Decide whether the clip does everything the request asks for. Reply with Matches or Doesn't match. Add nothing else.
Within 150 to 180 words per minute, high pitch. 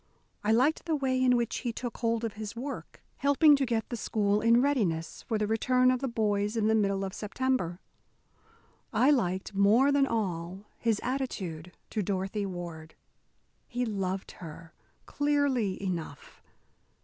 Matches